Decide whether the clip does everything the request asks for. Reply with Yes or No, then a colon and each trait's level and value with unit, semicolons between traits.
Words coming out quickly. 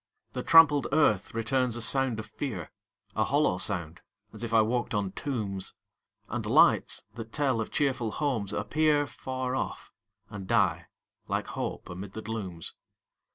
No: average, 155 wpm